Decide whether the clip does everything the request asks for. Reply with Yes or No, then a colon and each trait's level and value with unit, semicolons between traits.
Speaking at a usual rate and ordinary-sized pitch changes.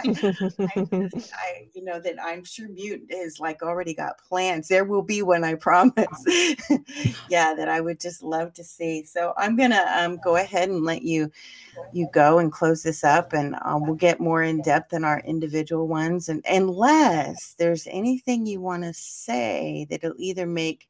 Yes: average, 185 wpm; average, 3.0 semitones